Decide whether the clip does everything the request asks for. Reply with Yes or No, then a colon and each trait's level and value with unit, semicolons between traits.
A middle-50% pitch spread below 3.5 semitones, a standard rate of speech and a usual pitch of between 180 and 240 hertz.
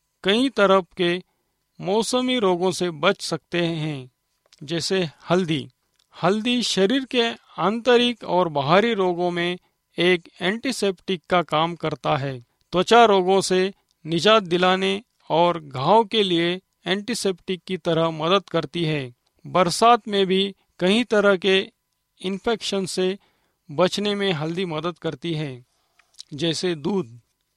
Yes: average, 3.0 semitones; average, 120 wpm; medium, 185 Hz